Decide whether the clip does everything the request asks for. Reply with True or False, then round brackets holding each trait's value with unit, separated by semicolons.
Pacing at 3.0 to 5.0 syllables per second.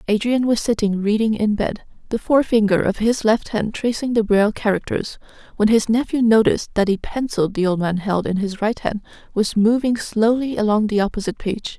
False (5.4 syllables/s)